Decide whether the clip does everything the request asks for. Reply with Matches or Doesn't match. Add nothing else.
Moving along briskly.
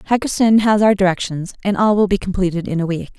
Matches